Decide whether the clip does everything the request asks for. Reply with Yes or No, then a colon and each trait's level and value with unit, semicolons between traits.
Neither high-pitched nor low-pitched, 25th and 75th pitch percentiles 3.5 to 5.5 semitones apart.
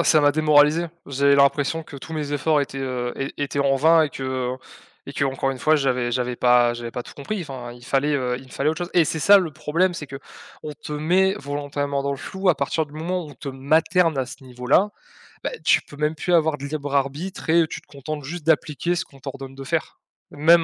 No: medium, 145 Hz; average, 2.9 semitones